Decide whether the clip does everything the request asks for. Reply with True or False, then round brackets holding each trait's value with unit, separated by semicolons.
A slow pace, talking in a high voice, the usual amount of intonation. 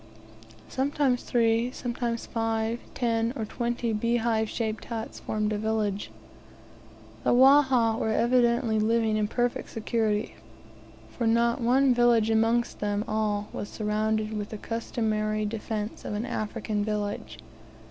False (125 wpm; 225 Hz; 1.8 semitones)